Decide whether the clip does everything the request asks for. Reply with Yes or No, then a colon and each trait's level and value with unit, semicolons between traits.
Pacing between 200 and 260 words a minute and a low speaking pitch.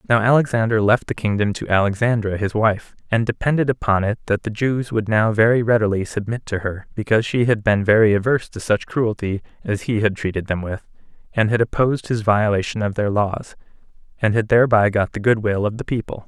Yes: fast, 205 wpm; low, 110 Hz